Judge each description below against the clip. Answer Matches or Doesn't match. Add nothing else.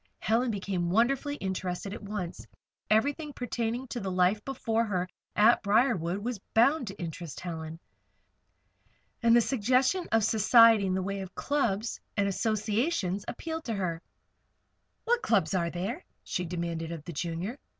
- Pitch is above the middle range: Matches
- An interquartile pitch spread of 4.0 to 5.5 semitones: Matches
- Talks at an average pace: Matches